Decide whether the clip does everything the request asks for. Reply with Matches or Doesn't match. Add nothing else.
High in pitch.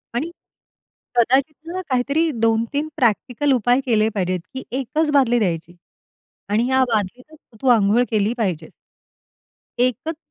Matches